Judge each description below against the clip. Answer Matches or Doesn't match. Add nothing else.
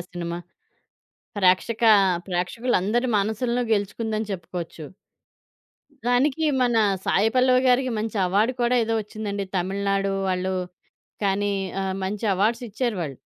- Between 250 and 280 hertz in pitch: Doesn't match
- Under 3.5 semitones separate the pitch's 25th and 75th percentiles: Doesn't match